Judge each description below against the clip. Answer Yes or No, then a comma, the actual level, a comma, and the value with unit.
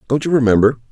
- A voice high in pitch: No, low, 125 Hz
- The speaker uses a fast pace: No, average, 195 wpm